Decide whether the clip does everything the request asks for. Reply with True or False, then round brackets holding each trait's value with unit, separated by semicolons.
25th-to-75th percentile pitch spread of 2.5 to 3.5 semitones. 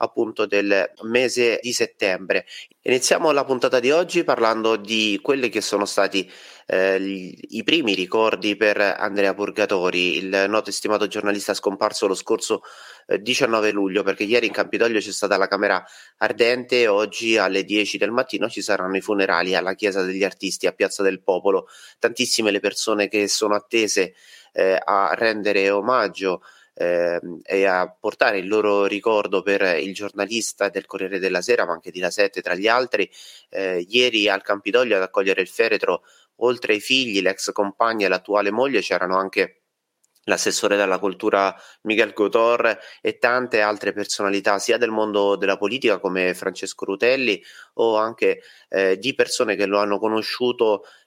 True (2.8 semitones)